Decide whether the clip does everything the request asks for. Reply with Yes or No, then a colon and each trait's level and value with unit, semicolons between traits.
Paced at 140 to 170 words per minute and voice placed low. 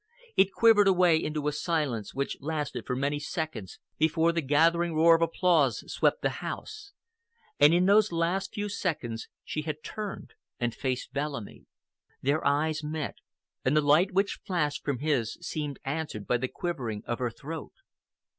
No: average, 165 wpm; medium, 155 Hz